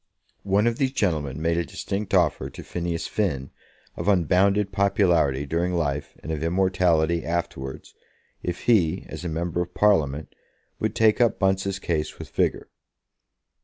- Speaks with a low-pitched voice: Yes, very low, 85 Hz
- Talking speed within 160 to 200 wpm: No, average, 150 wpm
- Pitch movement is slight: No, average, 3.7 semitones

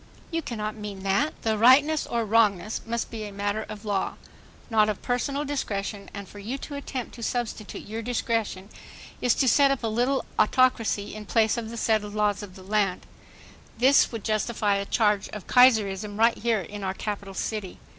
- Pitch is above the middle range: Yes, high, 215 Hz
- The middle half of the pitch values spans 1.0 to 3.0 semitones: Yes, average, 2.7 semitones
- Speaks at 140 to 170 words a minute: No, average, 185 wpm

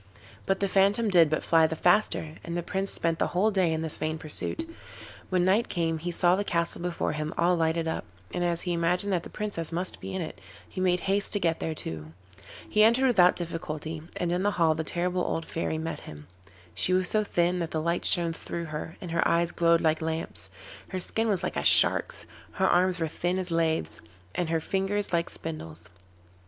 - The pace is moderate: No, fast, 220 wpm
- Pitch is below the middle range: No, medium, 170 Hz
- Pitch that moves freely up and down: No, narrow, 2.5 semitones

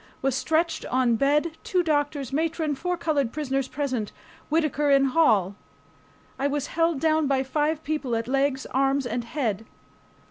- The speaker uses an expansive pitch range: No, average, 3.0 semitones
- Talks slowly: No, average, 150 wpm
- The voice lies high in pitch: Yes, very high, 285 Hz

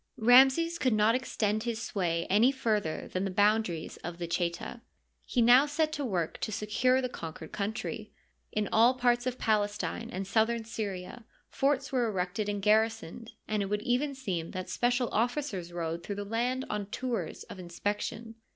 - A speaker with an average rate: Yes, average, 175 wpm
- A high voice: Yes, high, 220 Hz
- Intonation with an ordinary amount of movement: Yes, average, 4.0 semitones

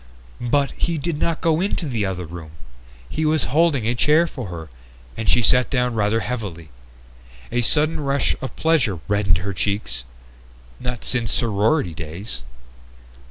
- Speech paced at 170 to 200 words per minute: No, average, 155 wpm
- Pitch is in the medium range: No, low, 120 Hz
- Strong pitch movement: Yes, wide, 7.0 semitones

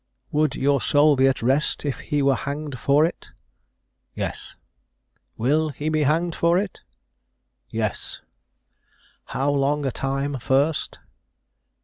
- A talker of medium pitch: Yes, medium, 145 Hz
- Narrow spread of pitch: Yes, narrow, 2.1 semitones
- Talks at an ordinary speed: No, slow, 125 wpm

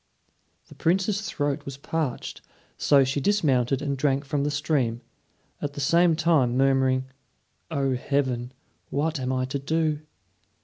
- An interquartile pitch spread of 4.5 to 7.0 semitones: No, average, 2.8 semitones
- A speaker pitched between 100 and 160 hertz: Yes, medium, 140 Hz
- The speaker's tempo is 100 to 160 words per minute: Yes, average, 140 wpm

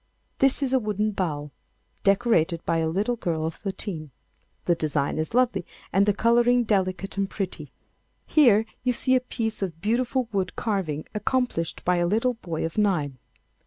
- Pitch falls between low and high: No, high, 200 Hz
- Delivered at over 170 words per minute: No, average, 165 wpm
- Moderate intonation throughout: No, wide, 5.9 semitones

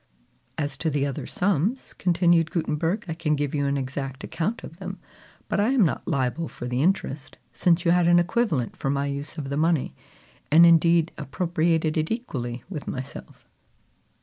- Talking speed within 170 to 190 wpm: Yes, average, 175 wpm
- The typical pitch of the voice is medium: Yes, medium, 160 Hz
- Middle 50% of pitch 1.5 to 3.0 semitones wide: No, average, 3.7 semitones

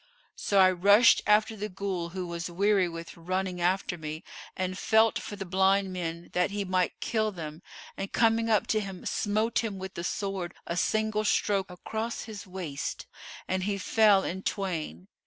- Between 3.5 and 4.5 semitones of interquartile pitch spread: No, average, 2.8 semitones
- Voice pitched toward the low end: No, high, 190 Hz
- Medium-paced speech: Yes, average, 175 wpm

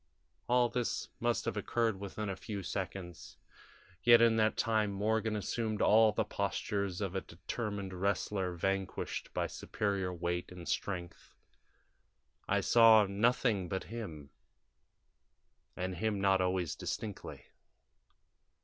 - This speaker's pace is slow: Yes, slow, 120 wpm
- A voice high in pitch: No, low, 100 Hz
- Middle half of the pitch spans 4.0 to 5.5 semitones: No, average, 3.0 semitones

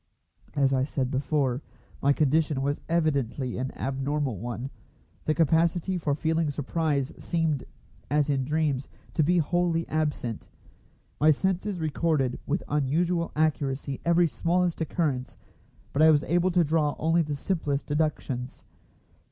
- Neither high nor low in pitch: Yes, medium, 150 Hz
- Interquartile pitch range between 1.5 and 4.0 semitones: Yes, average, 3.2 semitones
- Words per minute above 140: No, slow, 135 wpm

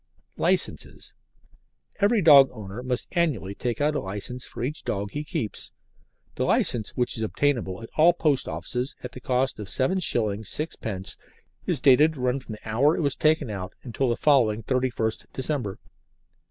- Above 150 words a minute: Yes, average, 165 wpm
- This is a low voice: Yes, low, 125 Hz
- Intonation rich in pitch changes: No, average, 4.9 semitones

